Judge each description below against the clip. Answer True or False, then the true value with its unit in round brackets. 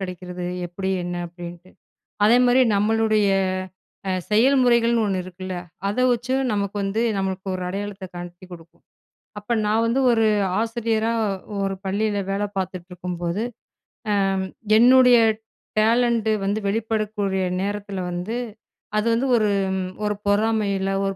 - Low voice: False (205 Hz)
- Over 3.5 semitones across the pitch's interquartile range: False (3.2 semitones)